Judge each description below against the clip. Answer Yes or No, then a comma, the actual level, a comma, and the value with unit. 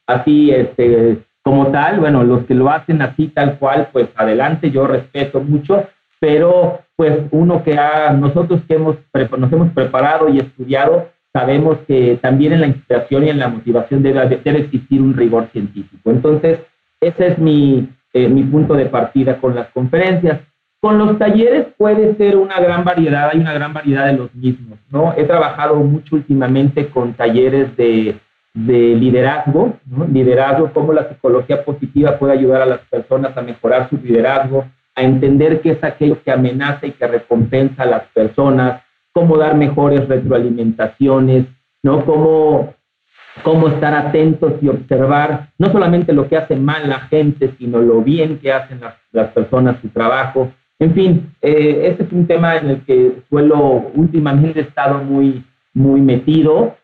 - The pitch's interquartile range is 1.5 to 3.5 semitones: Yes, average, 3.2 semitones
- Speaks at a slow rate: No, average, 165 wpm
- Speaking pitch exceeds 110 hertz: Yes, medium, 140 Hz